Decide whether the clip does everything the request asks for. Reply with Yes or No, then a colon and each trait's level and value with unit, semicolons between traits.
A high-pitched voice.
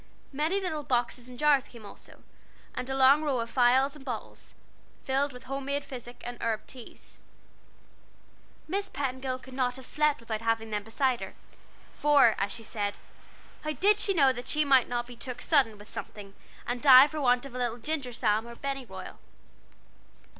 Yes: very high, 255 Hz